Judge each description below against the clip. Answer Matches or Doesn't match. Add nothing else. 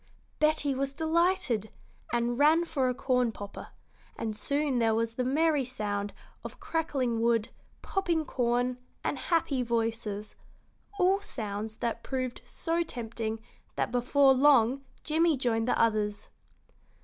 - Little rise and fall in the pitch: Doesn't match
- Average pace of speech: Doesn't match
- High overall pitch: Matches